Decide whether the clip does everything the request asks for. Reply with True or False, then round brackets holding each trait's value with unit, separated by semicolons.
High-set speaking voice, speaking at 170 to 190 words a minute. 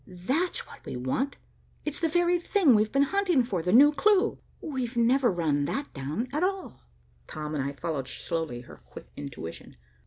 True (240 Hz; 180 wpm)